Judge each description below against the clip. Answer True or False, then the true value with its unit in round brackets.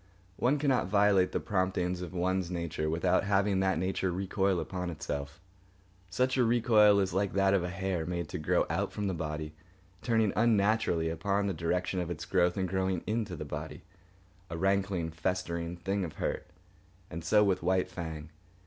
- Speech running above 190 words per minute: False (175 wpm)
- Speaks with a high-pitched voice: False (95 Hz)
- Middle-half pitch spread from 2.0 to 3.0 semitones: True (2.5 semitones)